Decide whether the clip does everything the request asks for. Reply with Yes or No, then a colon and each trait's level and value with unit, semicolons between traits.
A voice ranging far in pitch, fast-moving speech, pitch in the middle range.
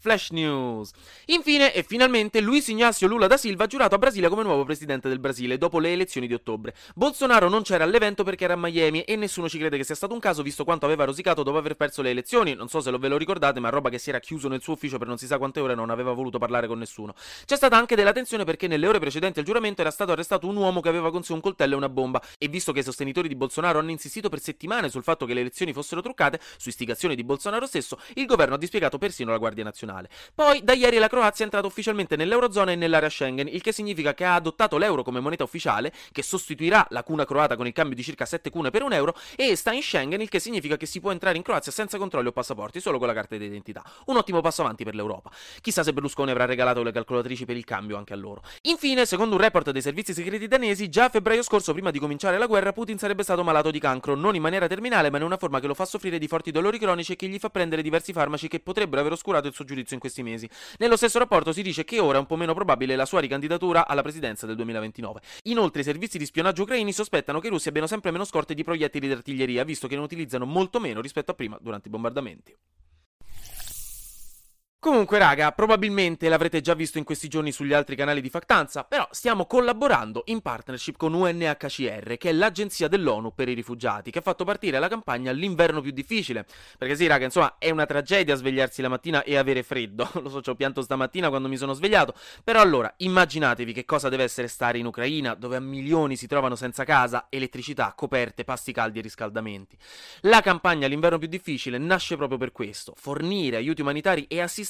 Yes: wide, 6.7 semitones; fast, 235 wpm; medium, 155 Hz